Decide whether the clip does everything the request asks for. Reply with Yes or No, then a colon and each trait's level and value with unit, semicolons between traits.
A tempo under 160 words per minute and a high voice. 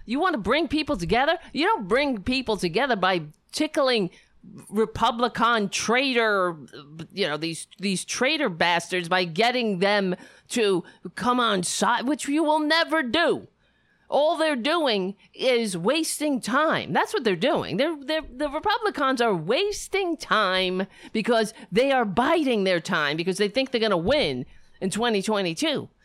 Yes: average, 150 wpm; high, 235 Hz